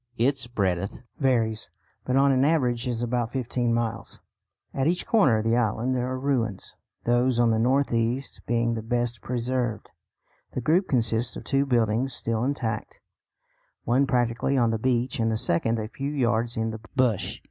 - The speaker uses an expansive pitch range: No, narrow, 2.4 semitones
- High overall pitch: No, low, 120 Hz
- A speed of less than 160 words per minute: No, average, 175 wpm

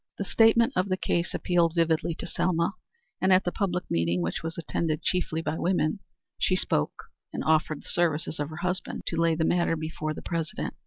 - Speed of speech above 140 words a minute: Yes, average, 200 wpm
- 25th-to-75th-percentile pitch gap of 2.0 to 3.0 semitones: Yes, narrow, 2.5 semitones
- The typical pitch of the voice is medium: Yes, medium, 170 Hz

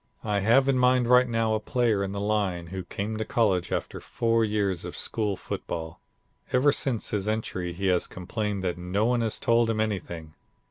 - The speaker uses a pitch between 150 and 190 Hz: No, low, 105 Hz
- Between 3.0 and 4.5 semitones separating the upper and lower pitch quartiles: Yes, average, 3.5 semitones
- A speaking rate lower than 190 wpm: No, average, 195 wpm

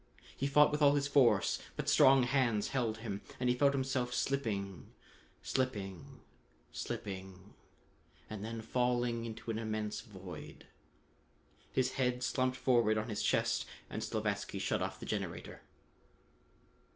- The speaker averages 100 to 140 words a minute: Yes, slow, 135 wpm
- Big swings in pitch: No, average, 3.5 semitones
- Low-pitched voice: Yes, low, 120 Hz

